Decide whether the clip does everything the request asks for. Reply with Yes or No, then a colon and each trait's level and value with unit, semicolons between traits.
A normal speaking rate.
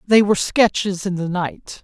Yes: average, 195 wpm